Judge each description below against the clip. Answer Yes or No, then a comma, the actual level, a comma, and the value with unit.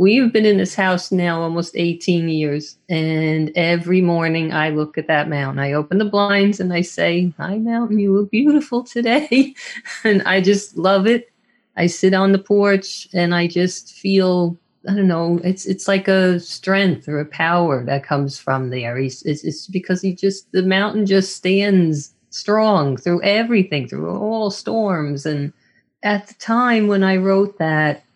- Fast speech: No, average, 175 wpm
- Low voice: No, medium, 185 Hz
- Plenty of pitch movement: No, average, 3.8 semitones